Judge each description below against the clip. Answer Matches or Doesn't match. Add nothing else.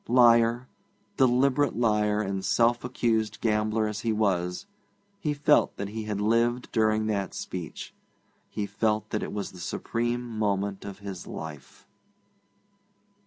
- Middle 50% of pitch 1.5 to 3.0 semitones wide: Matches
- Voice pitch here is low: Matches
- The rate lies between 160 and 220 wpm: Doesn't match